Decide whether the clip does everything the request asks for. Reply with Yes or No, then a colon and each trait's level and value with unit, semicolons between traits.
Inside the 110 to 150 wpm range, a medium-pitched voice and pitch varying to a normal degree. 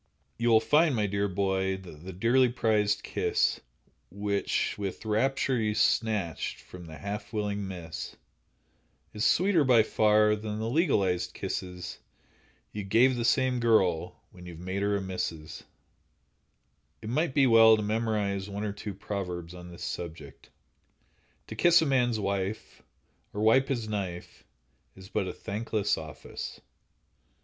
No: average, 145 wpm; low, 105 Hz; average, 3.3 semitones